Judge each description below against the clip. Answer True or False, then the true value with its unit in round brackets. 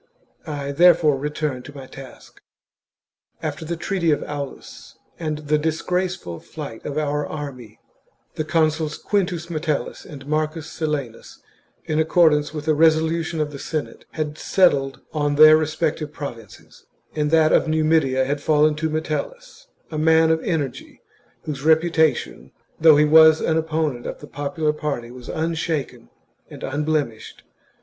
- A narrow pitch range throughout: True (1.8 semitones)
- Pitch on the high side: False (155 Hz)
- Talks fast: False (145 wpm)